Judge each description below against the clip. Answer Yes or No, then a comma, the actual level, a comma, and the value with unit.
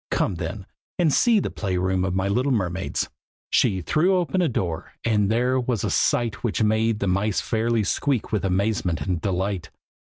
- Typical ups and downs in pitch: Yes, average, 4.5 semitones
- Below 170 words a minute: No, average, 185 wpm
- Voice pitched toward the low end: Yes, low, 105 Hz